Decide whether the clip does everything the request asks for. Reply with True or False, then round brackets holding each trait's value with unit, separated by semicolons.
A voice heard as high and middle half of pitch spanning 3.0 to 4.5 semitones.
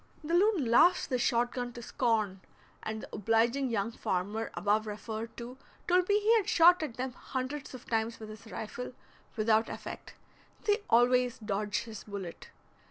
True (235 Hz; 3.6 semitones)